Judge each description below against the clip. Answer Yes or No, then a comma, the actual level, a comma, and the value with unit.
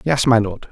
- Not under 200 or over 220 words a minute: No, fast, 250 wpm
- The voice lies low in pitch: Yes, low, 120 Hz